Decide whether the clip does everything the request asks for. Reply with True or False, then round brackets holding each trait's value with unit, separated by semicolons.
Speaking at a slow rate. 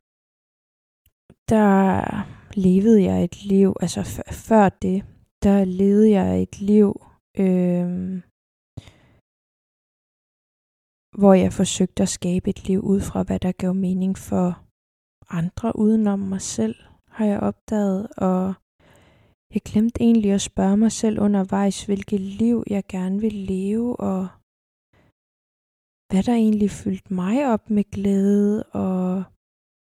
True (125 wpm)